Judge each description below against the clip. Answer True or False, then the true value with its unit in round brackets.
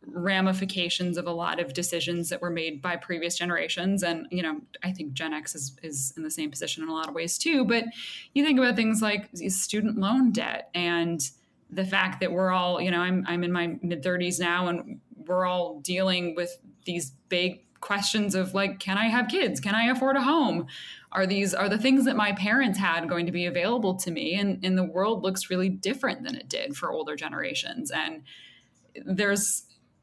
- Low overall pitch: False (185 Hz)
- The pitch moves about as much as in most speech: True (3.0 semitones)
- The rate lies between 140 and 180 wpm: False (205 wpm)